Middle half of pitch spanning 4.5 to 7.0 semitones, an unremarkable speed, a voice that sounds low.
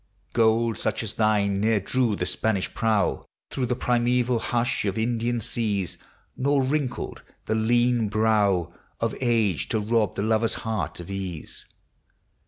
No: average, 2.7 semitones; average, 145 wpm; low, 110 Hz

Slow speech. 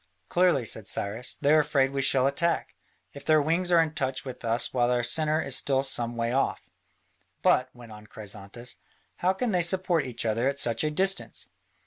No: average, 195 wpm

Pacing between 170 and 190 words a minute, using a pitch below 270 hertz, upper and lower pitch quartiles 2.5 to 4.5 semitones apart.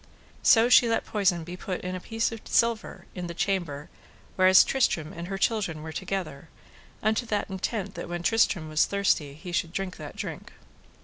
Yes: average, 185 wpm; medium, 185 Hz; average, 3.7 semitones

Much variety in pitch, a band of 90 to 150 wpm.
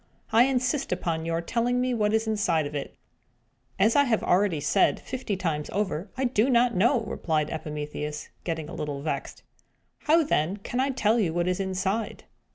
No: wide, 6.8 semitones; average, 180 wpm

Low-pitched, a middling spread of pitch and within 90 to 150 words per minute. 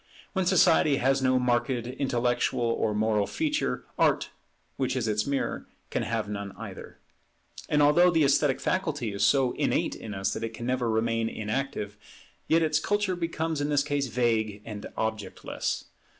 No: low, 130 Hz; average, 5.0 semitones; average, 165 wpm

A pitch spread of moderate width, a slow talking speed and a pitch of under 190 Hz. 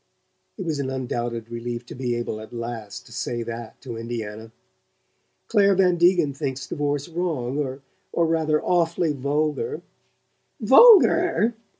No: wide, 6.3 semitones; slow, 130 wpm; medium, 140 Hz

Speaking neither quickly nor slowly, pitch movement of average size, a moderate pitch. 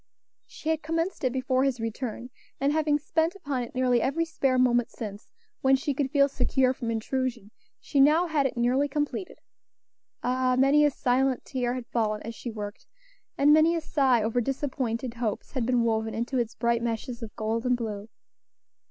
No: average, 185 wpm; average, 3.3 semitones; very high, 255 Hz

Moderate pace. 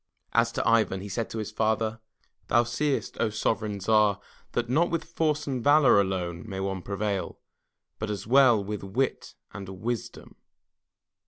Yes: average, 160 wpm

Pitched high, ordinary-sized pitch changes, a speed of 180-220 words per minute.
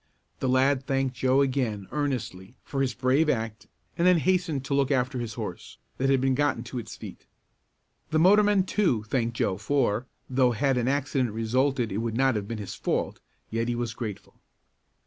No: low, 130 Hz; average, 3.3 semitones; average, 185 wpm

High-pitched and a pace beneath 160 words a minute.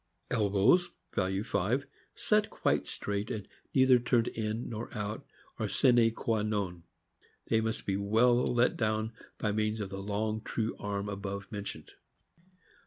No: low, 110 Hz; average, 150 wpm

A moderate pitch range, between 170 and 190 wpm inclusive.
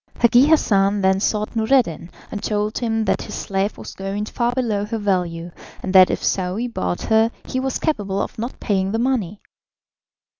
Yes: average, 3.4 semitones; average, 180 wpm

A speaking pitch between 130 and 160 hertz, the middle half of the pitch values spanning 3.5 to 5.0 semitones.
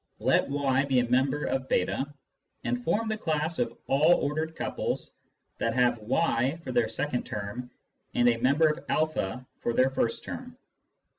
Yes: low, 135 Hz; average, 4.0 semitones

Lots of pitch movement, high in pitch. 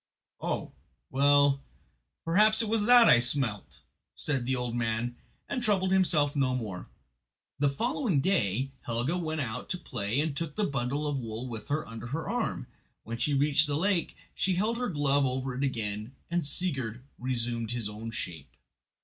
No: wide, 5.7 semitones; medium, 140 Hz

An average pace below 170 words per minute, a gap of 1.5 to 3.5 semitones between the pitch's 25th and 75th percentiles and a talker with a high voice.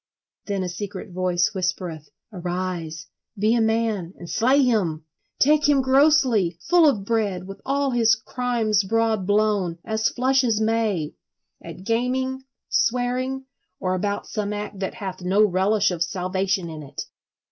No: average, 145 wpm; average, 4.6 semitones; high, 210 Hz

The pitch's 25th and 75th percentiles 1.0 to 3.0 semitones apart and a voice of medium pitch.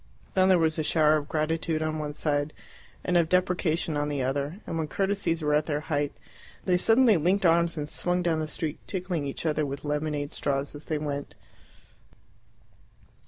Yes: narrow, 2.6 semitones; medium, 155 Hz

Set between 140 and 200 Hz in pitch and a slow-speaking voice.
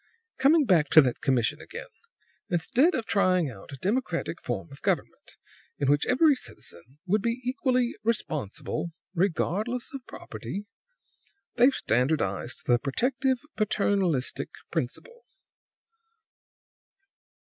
Yes: medium, 185 Hz; slow, 110 wpm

